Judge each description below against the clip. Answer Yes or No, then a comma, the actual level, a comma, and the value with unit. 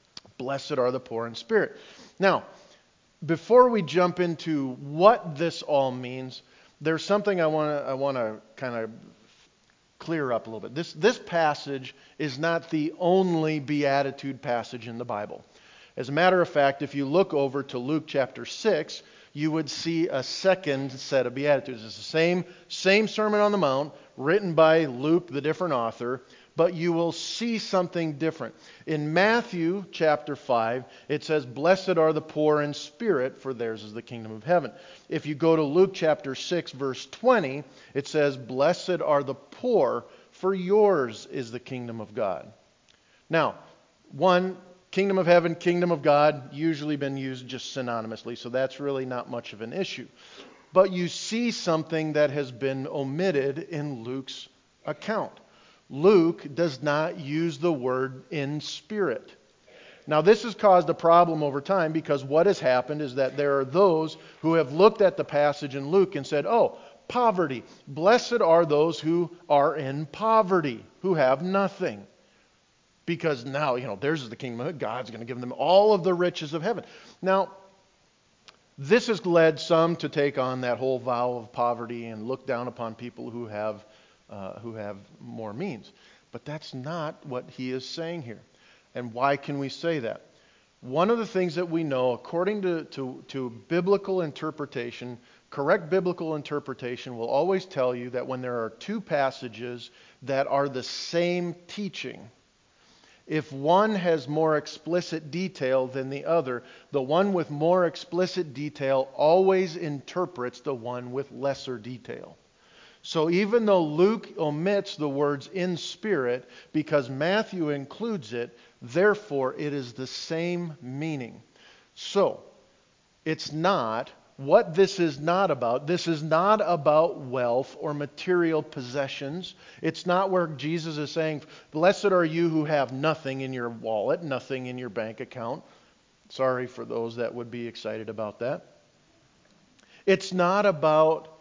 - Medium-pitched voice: Yes, medium, 150 Hz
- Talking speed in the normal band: Yes, average, 160 wpm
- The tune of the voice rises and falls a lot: No, average, 5.0 semitones